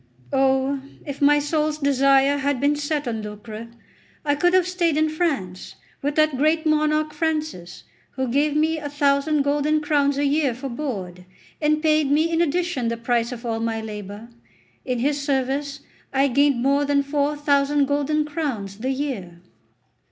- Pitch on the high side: Yes, very high, 285 Hz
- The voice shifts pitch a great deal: No, average, 2.9 semitones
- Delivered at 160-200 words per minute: Yes, average, 165 wpm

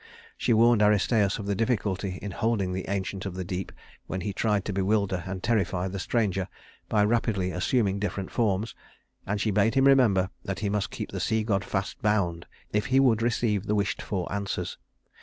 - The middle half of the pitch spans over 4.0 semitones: No, narrow, 2.6 semitones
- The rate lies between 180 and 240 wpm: Yes, average, 195 wpm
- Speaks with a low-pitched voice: Yes, low, 100 Hz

